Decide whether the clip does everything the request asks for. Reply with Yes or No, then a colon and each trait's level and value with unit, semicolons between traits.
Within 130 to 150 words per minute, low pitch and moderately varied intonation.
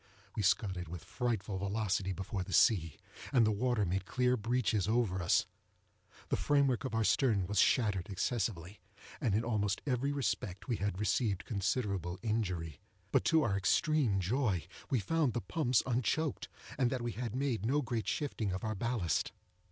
No: average, 170 wpm; low, 110 Hz; average, 4.5 semitones